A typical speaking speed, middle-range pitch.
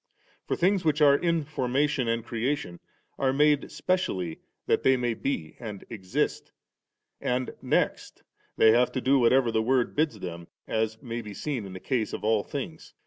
No: average, 180 wpm; low, 125 Hz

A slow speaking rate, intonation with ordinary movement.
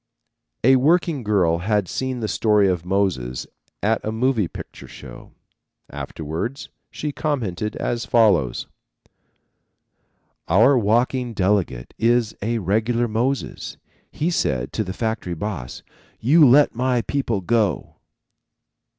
Yes: slow, 115 wpm; average, 5.0 semitones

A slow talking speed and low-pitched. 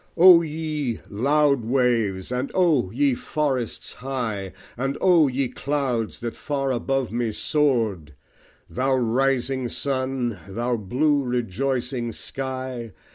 Yes: slow, 115 wpm; low, 130 Hz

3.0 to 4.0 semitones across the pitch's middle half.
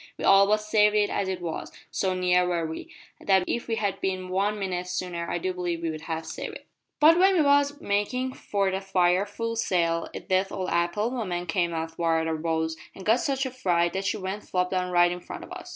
Yes: average, 3.3 semitones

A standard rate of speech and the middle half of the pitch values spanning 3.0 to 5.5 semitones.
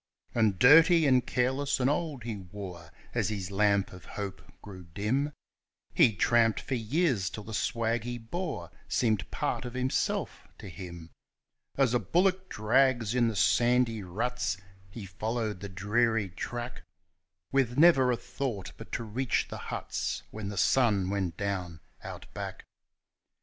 Yes: average, 150 wpm; average, 4.1 semitones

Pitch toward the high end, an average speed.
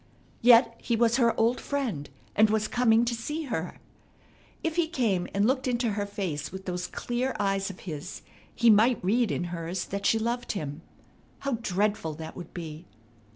Yes: high, 215 Hz; average, 180 wpm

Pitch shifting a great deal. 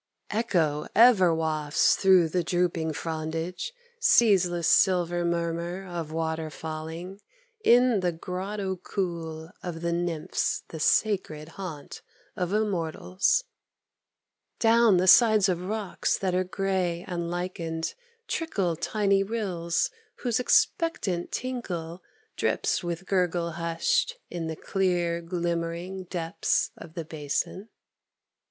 No: average, 2.8 semitones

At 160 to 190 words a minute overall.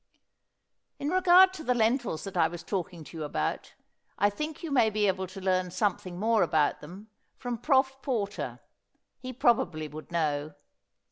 Yes: average, 165 wpm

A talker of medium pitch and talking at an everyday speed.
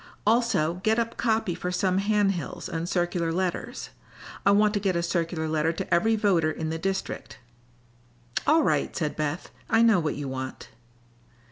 Yes: medium, 180 Hz; average, 170 wpm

